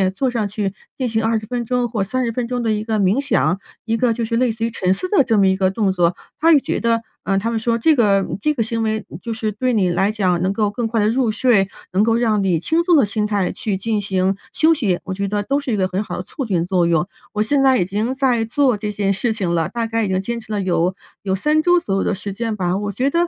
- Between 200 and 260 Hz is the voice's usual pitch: Yes, high, 220 Hz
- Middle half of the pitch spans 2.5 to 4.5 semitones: Yes, average, 3.5 semitones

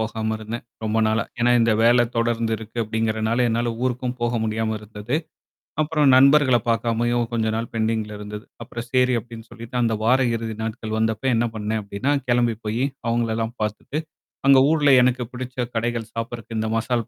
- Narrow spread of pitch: Yes, narrow, 1.6 semitones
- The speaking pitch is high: No, low, 115 Hz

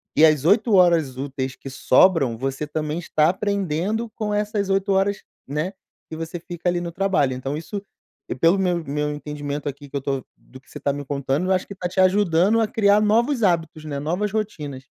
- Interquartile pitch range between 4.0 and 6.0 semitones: Yes, wide, 5.4 semitones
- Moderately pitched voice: Yes, medium, 165 Hz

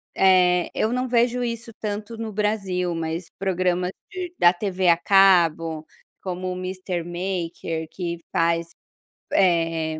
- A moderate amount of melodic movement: Yes, average, 3.2 semitones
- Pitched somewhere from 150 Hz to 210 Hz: Yes, medium, 185 Hz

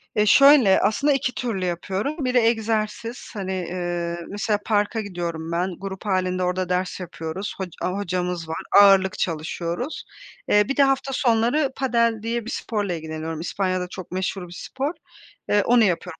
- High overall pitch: Yes, high, 195 Hz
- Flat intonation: No, average, 4.3 semitones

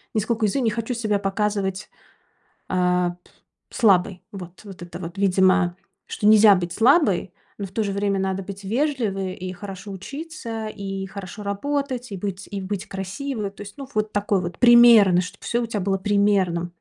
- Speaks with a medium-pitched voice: No, high, 200 Hz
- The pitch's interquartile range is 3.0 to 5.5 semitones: No, narrow, 2.6 semitones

